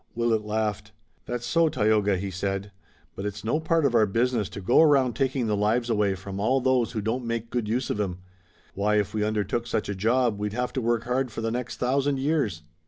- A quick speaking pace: Yes, fast, 225 wpm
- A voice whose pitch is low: Yes, low, 115 Hz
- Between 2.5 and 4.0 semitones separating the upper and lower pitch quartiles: Yes, average, 3.3 semitones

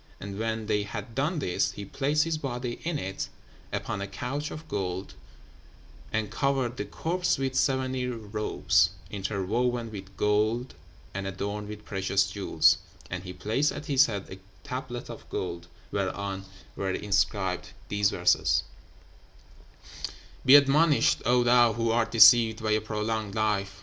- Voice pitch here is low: Yes, low, 110 Hz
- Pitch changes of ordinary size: Yes, average, 4.2 semitones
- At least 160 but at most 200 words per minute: No, average, 145 wpm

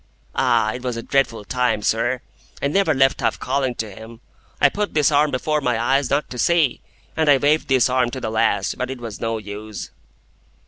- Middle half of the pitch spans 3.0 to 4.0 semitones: Yes, average, 3.6 semitones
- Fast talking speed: Yes, fast, 210 wpm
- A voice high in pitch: No, low, 130 Hz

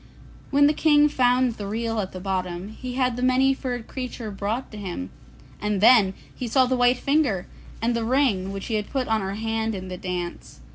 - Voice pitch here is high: Yes, high, 225 Hz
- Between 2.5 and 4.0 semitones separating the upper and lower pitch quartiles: No, average, 4.5 semitones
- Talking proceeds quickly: Yes, fast, 210 wpm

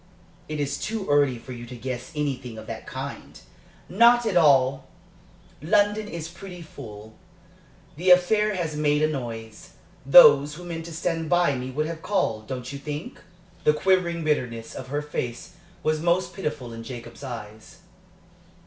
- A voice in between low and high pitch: Yes, medium, 150 Hz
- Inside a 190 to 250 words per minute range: No, average, 160 wpm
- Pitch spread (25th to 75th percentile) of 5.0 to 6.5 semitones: Yes, average, 5.3 semitones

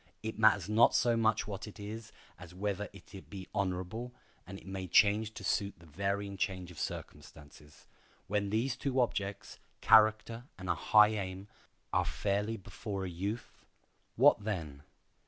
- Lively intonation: No, average, 2.8 semitones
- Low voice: Yes, low, 100 Hz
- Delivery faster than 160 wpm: No, average, 150 wpm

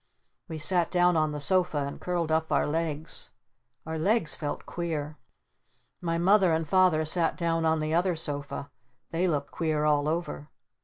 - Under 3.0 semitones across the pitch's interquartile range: Yes, narrow, 2.4 semitones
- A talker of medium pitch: Yes, medium, 160 Hz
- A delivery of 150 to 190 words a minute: Yes, average, 165 wpm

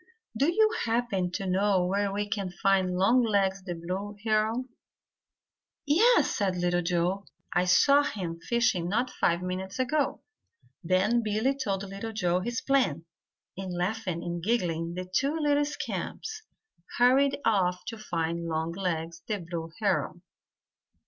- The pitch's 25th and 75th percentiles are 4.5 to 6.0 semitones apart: Yes, average, 4.9 semitones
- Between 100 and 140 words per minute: Yes, slow, 135 wpm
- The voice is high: Yes, high, 195 Hz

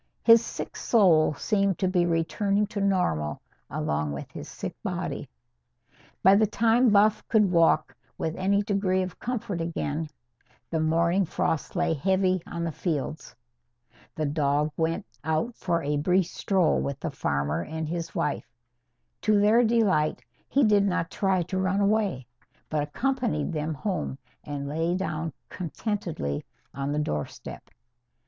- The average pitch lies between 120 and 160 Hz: No, medium, 175 Hz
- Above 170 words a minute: No, average, 145 wpm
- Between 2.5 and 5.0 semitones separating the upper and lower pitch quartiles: Yes, average, 4.5 semitones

